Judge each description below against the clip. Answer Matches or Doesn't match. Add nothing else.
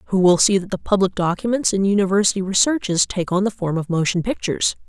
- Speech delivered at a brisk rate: Matches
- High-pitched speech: Matches